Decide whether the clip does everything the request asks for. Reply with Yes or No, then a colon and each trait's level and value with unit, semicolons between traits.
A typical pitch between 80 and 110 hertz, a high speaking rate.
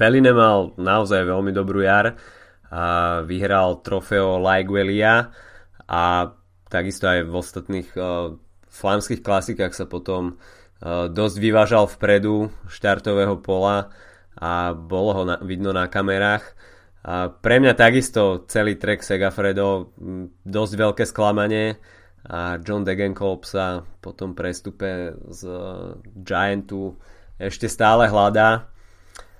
No: very low, 95 Hz; slow, 110 wpm